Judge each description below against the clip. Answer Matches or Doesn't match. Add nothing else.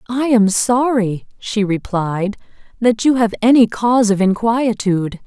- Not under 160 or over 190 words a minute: Doesn't match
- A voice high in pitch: Matches